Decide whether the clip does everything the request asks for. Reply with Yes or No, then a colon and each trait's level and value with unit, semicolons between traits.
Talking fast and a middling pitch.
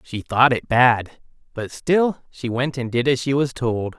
No: fast, 210 wpm; low, 125 Hz